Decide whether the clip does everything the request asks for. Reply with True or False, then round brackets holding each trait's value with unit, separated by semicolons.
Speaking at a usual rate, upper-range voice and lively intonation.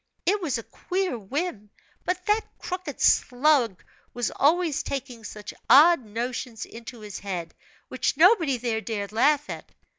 True (145 wpm; 255 Hz; 6.9 semitones)